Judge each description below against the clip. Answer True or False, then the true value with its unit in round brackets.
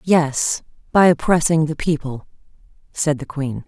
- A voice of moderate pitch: True (155 Hz)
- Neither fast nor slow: False (130 wpm)